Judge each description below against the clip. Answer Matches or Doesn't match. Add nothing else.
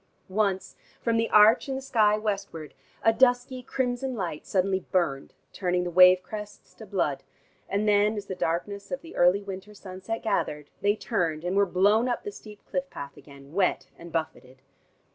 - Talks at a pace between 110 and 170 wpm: Doesn't match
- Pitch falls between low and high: Doesn't match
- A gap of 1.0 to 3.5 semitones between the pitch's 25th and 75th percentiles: Doesn't match